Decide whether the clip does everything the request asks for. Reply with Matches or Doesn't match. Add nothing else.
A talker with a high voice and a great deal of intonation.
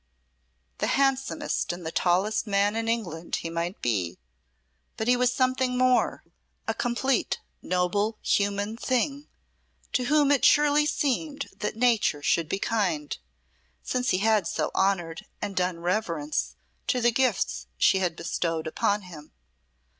Matches